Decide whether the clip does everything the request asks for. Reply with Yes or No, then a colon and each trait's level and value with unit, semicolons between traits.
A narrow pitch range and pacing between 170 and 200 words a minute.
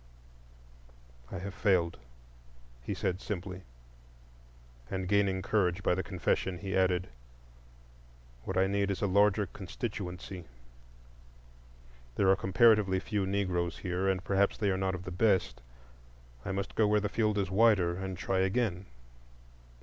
No: narrow, 1.7 semitones; average, 140 wpm